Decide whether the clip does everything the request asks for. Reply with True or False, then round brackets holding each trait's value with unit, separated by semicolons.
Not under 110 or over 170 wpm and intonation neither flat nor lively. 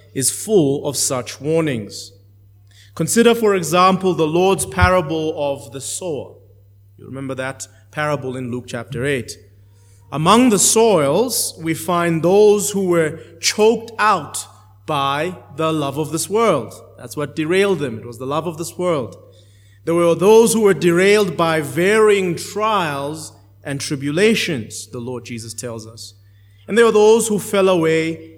False (150 wpm; 8.5 semitones)